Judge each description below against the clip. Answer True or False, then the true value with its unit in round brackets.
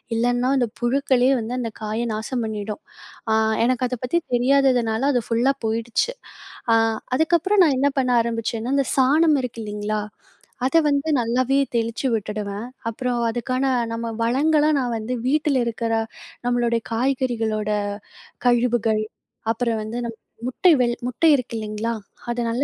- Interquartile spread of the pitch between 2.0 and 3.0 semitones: True (2.7 semitones)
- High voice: True (240 Hz)